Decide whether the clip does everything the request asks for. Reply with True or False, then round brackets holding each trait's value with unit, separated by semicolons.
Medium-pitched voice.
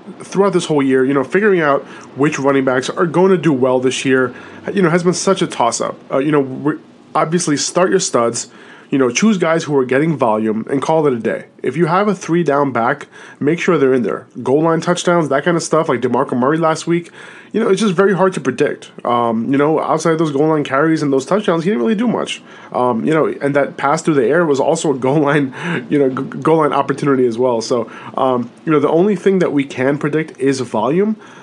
True (150 Hz)